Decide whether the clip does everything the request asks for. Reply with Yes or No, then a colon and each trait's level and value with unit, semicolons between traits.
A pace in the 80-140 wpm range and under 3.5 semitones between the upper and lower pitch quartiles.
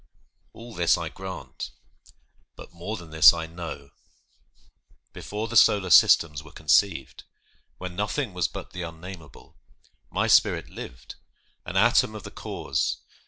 No: slow, 135 wpm; average, 4.2 semitones